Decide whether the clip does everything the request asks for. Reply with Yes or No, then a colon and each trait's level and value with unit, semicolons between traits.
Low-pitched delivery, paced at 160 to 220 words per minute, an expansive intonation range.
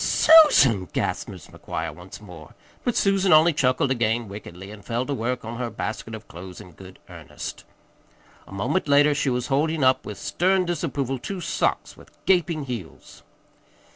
Yes: low, 125 Hz; average, 170 wpm; wide, 6.9 semitones